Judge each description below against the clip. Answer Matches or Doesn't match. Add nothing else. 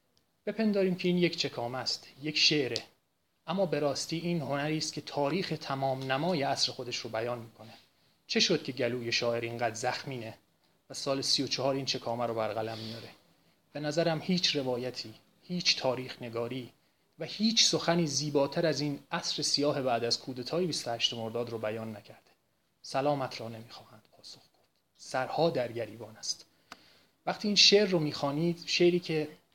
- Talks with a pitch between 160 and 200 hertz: Doesn't match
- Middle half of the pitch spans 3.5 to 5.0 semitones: Doesn't match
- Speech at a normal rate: Doesn't match